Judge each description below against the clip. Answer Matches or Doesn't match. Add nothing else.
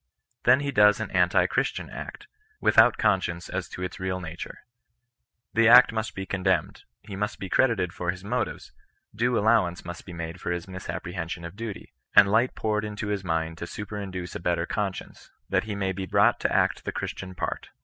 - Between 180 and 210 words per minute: Matches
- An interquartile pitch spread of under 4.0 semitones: Matches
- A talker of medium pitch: Doesn't match